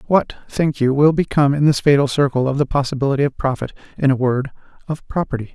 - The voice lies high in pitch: No, medium, 140 Hz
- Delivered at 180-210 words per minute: Yes, average, 195 wpm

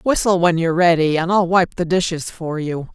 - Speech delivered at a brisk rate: Yes, fast, 225 wpm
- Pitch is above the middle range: No, medium, 170 Hz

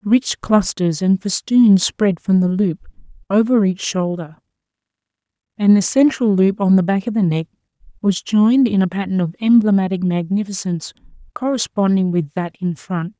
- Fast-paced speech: No, average, 155 wpm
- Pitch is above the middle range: Yes, high, 195 Hz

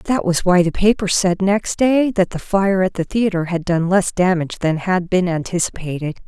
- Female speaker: Yes, female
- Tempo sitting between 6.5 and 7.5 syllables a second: No, 4.9 syllables/s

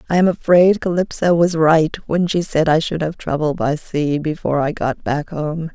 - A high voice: No, medium, 160 Hz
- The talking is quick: Yes, fast, 210 wpm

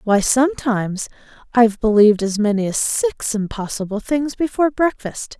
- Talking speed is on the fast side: No, slow, 135 wpm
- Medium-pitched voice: No, high, 235 Hz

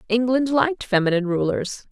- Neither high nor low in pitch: No, high, 220 Hz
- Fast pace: No, slow, 125 wpm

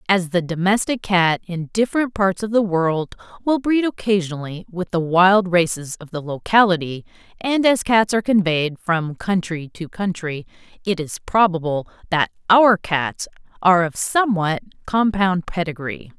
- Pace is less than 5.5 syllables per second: Yes, 4.6 syllables/s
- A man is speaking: No, female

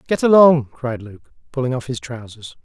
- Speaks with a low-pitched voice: Yes, low, 125 Hz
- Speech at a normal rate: Yes, average, 180 wpm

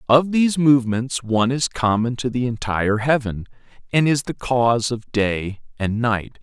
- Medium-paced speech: Yes, average, 170 wpm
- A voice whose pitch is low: Yes, low, 120 Hz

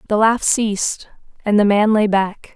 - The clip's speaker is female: Yes, female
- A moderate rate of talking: Yes, average, 190 wpm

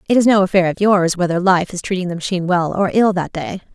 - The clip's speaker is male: No, female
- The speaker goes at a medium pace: No, fast, 270 wpm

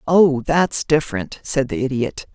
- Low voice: No, medium, 145 Hz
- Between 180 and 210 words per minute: No, average, 155 wpm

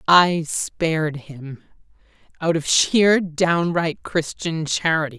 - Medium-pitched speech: Yes, medium, 160 Hz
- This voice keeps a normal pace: No, slow, 95 wpm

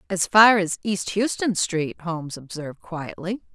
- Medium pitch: Yes, medium, 180 Hz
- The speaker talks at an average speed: Yes, average, 150 wpm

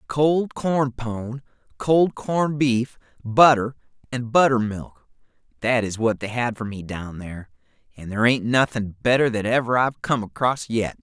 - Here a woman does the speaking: No, male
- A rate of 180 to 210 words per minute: No, average, 160 wpm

